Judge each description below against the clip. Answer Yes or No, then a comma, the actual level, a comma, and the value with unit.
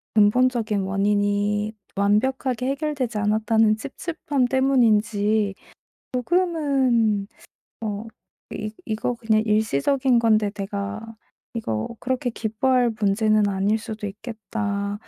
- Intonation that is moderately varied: Yes, average, 3.4 semitones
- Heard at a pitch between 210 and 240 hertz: Yes, high, 220 Hz